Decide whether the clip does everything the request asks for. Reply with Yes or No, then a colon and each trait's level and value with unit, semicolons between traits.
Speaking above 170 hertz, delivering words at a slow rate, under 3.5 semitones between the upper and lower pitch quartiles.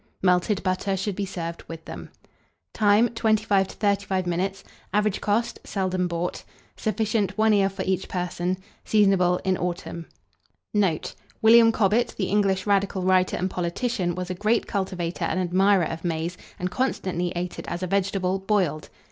No: high, 190 Hz; average, 155 wpm; narrow, 2.4 semitones